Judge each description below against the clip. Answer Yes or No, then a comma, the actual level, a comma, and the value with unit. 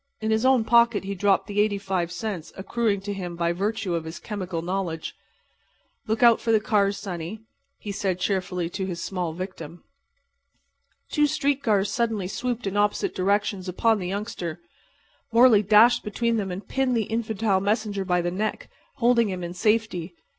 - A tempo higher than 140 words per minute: Yes, average, 170 wpm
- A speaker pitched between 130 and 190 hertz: No, high, 200 Hz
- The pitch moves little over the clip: No, average, 3.4 semitones